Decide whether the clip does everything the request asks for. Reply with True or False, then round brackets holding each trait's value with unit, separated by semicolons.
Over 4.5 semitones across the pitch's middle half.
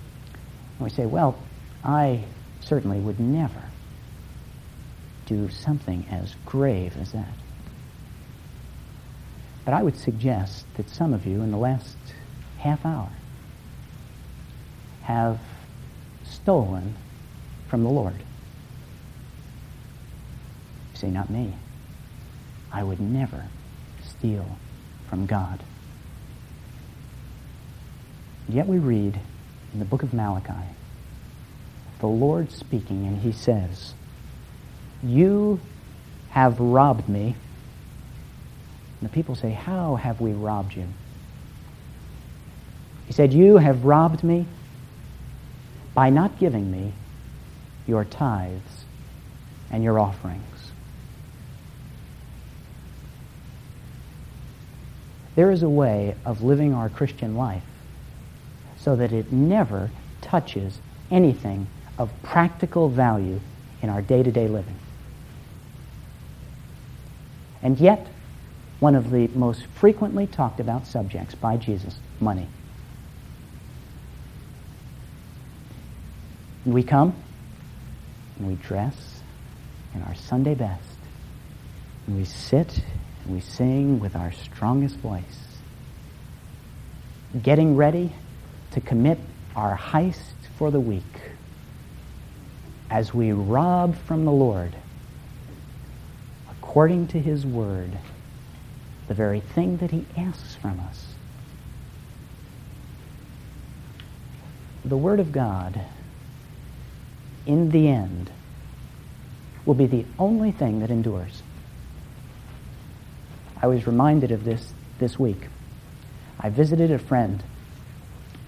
True (5.3 semitones)